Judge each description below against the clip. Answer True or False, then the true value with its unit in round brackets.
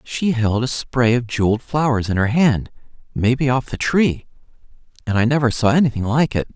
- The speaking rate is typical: True (190 wpm)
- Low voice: True (125 Hz)